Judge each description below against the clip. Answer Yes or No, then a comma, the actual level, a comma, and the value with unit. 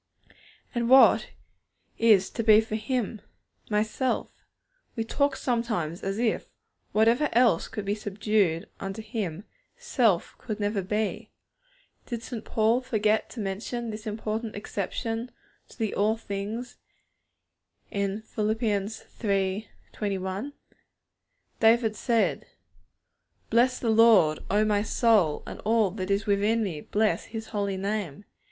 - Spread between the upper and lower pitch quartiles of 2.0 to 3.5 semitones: Yes, narrow, 2.4 semitones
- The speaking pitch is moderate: No, high, 215 Hz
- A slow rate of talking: Yes, slow, 125 wpm